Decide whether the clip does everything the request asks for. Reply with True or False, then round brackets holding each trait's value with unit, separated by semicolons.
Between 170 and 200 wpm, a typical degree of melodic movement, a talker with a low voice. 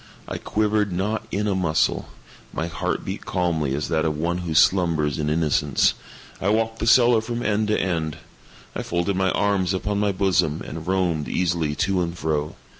True (185 wpm; 4.2 semitones; 90 Hz)